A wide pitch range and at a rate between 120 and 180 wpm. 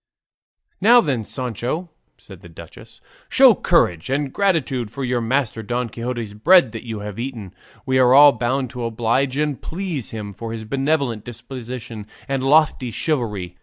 No: average, 3.6 semitones; average, 160 wpm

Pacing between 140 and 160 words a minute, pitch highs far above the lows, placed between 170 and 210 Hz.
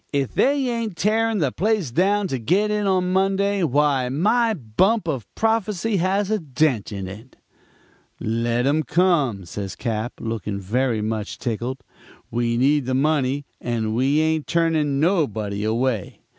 No: average, 150 wpm; wide, 8.4 semitones; medium, 145 Hz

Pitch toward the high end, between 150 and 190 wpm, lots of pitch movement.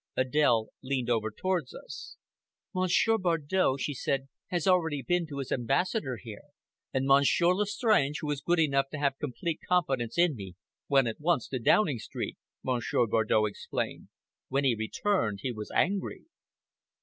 No: medium, 140 Hz; average, 155 wpm; wide, 5.9 semitones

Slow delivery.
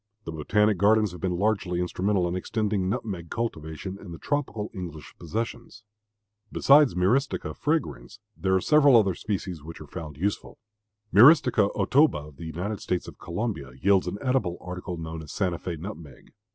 No: average, 165 wpm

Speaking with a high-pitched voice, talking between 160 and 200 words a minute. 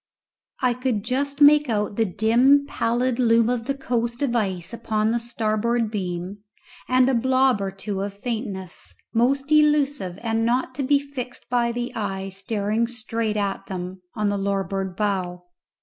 Yes: high, 230 Hz; average, 165 wpm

